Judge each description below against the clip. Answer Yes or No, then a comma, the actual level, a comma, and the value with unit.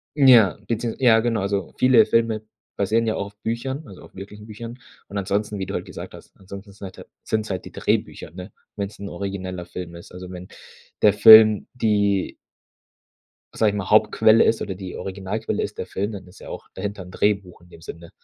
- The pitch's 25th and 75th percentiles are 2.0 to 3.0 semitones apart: Yes, narrow, 2.6 semitones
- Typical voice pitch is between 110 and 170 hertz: No, low, 100 Hz